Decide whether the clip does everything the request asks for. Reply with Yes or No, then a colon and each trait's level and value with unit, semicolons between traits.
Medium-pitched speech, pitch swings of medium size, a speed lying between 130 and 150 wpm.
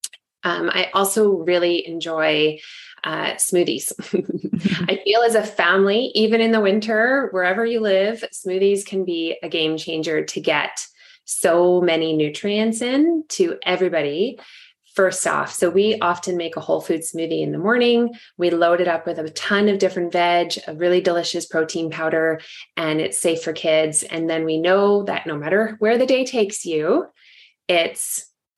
No: medium, 180 Hz; average, 4.4 semitones; average, 165 wpm